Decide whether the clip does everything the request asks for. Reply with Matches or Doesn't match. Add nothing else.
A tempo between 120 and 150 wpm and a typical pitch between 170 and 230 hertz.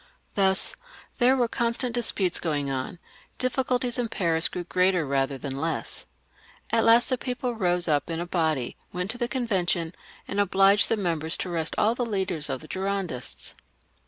Doesn't match